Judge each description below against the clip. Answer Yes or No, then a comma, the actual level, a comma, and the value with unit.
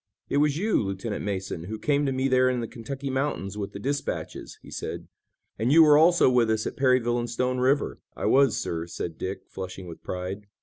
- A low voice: Yes, low, 120 Hz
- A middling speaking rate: No, fast, 215 wpm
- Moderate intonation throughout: No, wide, 5.7 semitones